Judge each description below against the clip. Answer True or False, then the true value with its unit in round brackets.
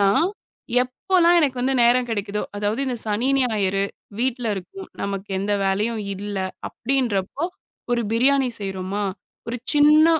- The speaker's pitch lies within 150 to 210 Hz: False (230 Hz)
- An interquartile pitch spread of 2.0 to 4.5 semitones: False (4.9 semitones)